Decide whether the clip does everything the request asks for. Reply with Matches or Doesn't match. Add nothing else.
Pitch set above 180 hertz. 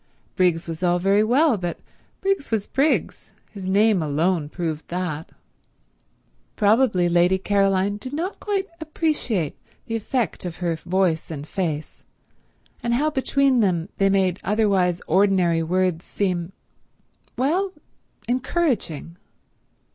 Matches